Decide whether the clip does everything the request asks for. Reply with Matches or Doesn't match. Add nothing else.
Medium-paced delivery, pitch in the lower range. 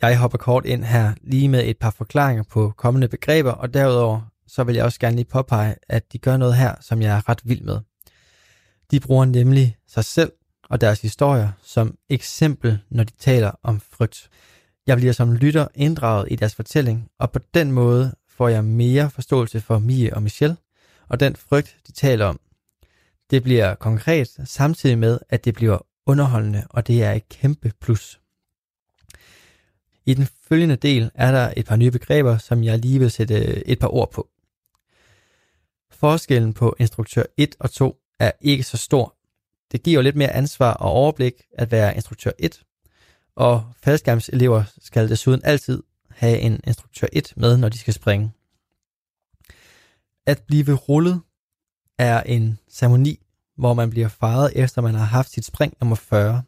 Matches